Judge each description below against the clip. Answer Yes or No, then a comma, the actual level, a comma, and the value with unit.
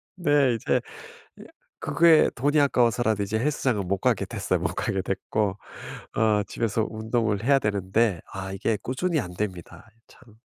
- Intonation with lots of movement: No, average, 4.2 semitones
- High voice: No, low, 110 Hz